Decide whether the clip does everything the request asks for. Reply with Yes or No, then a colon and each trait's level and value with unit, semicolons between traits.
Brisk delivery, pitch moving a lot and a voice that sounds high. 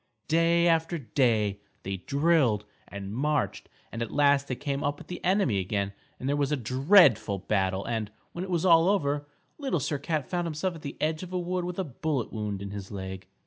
No: fast, 210 wpm; wide, 7.7 semitones; medium, 140 Hz